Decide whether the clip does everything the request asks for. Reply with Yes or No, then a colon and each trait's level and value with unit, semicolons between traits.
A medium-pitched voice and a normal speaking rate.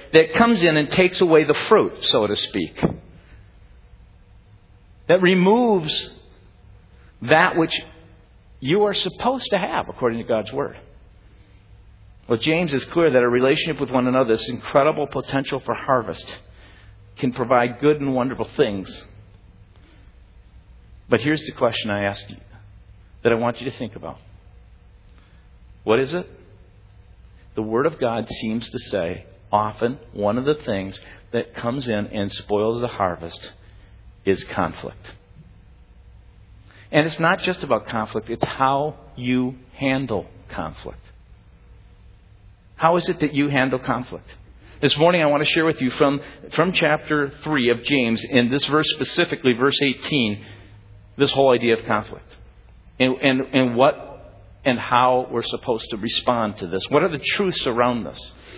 No: low, 120 Hz; average, 150 wpm